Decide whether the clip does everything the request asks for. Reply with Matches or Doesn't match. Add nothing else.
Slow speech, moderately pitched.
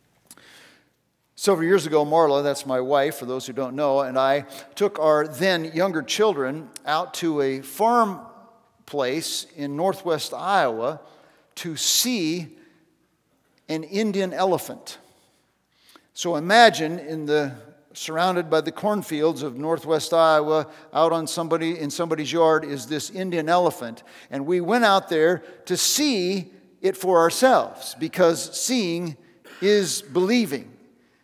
Matches